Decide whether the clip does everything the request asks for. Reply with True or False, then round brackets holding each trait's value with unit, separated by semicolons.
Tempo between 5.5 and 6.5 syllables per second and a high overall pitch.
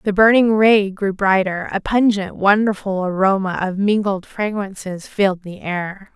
False (4.4 syllables/s; 200 Hz)